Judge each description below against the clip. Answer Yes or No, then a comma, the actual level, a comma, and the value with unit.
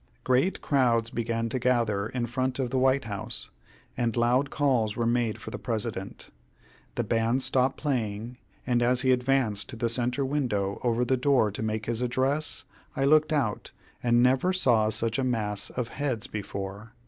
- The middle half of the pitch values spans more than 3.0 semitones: No, average, 2.7 semitones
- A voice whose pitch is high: No, low, 120 Hz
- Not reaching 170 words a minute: No, average, 175 wpm